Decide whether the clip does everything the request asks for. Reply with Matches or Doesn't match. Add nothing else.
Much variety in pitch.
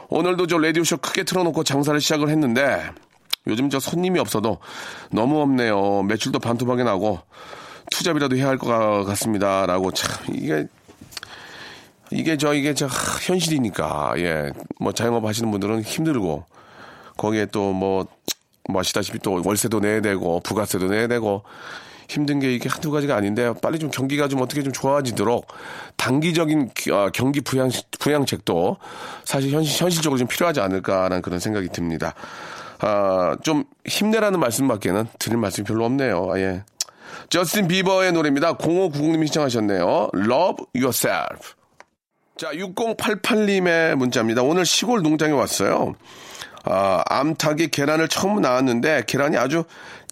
Matches